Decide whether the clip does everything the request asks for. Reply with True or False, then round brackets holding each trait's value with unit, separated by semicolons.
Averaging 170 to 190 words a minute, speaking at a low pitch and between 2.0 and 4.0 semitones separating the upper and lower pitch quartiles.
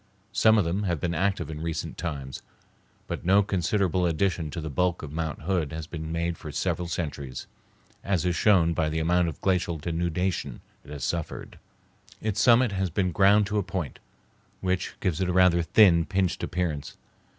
True (185 wpm; 85 Hz; 3.0 semitones)